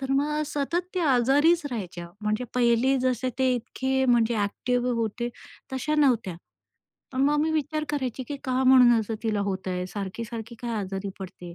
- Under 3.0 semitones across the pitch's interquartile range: No, average, 4.1 semitones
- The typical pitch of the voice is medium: No, high, 245 Hz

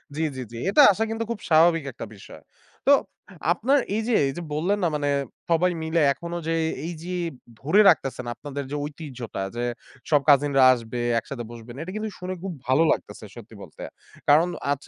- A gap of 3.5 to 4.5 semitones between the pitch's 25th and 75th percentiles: No, average, 5.1 semitones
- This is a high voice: No, medium, 155 Hz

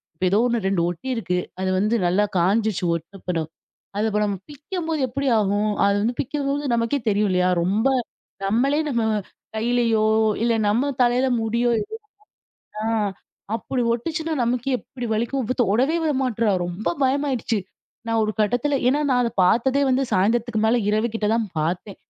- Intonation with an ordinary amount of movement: Yes, average, 4.2 semitones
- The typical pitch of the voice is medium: No, high, 230 Hz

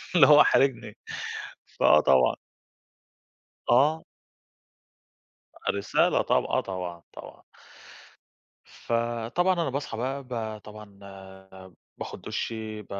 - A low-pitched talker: Yes, low, 110 Hz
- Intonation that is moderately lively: No, wide, 5.7 semitones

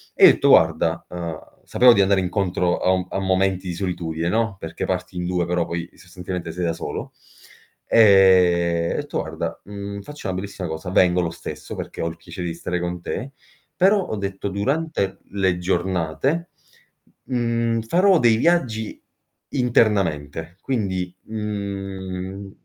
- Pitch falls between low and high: No, very low, 95 Hz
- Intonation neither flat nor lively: Yes, average, 3.3 semitones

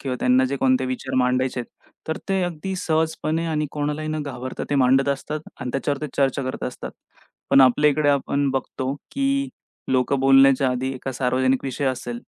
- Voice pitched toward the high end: No, low, 135 Hz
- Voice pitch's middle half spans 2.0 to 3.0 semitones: Yes, average, 2.7 semitones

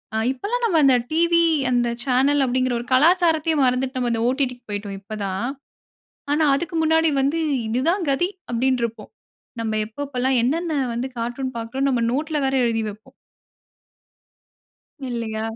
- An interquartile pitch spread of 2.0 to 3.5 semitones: No, average, 4.7 semitones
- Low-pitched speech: No, very high, 260 Hz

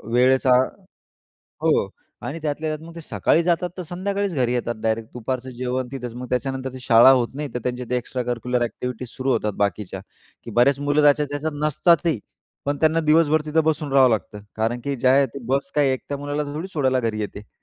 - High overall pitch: No, low, 130 Hz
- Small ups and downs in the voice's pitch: No, average, 3.5 semitones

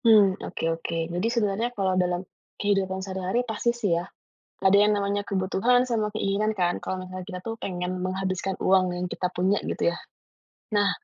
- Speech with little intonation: Yes, narrow, 2.1 semitones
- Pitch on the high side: Yes, high, 195 Hz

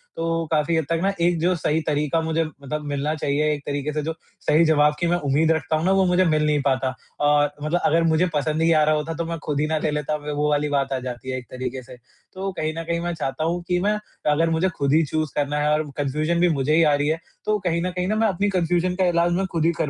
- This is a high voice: No, medium, 155 Hz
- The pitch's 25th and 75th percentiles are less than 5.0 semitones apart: Yes, narrow, 2.4 semitones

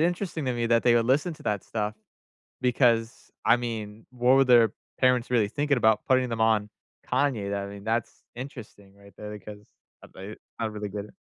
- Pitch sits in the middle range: No, low, 115 Hz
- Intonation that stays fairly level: No, average, 3.3 semitones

